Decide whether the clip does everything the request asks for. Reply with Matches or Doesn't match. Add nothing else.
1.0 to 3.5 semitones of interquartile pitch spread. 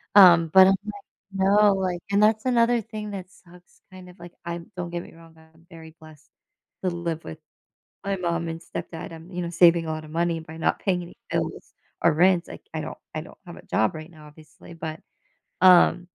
Matches